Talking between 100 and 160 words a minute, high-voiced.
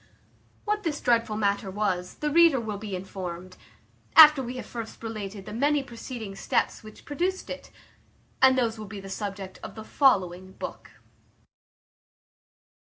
Yes: average, 150 wpm; high, 220 Hz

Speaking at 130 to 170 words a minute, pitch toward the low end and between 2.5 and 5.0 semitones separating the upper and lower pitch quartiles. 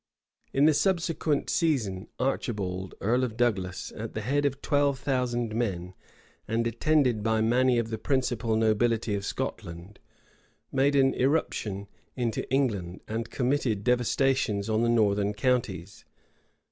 Yes: slow, 135 wpm; low, 115 Hz; average, 4.1 semitones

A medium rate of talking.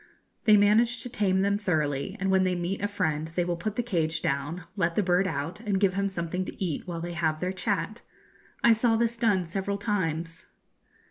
No: fast, 210 wpm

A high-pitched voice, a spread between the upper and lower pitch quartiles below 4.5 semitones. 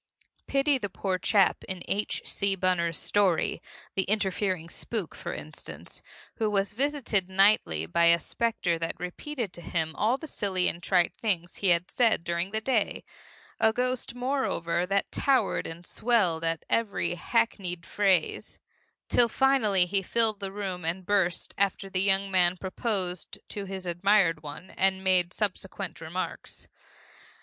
Yes: high, 195 Hz; average, 3.4 semitones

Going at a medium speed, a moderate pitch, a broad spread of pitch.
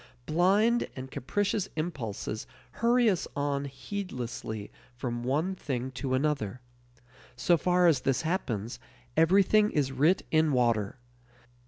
No: slow, 120 wpm; medium, 145 Hz; wide, 6.3 semitones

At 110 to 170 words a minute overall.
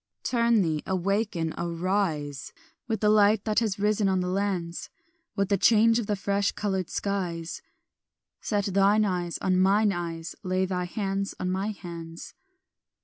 Yes: average, 150 wpm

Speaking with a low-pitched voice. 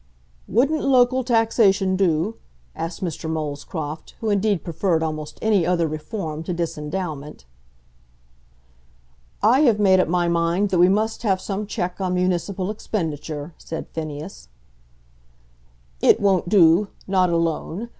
No: medium, 180 Hz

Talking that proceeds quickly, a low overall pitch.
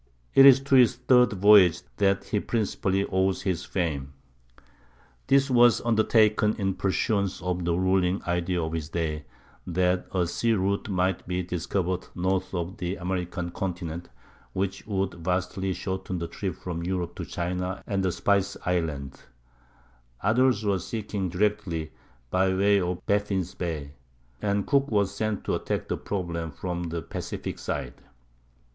No: average, 150 wpm; very low, 95 Hz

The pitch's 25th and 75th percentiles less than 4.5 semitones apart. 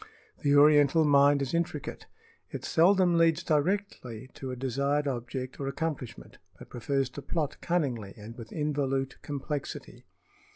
Yes: average, 2.8 semitones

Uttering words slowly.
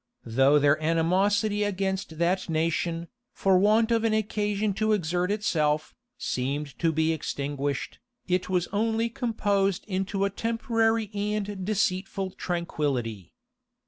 Yes: slow, 120 wpm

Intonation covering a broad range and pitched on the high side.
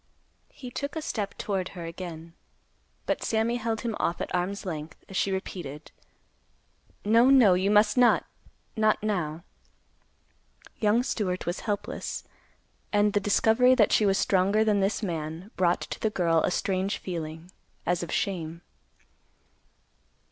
No: average, 3.8 semitones; high, 195 Hz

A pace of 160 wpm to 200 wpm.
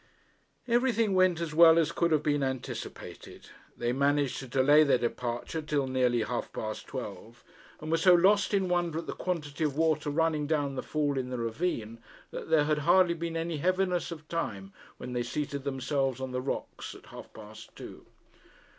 Yes: average, 185 wpm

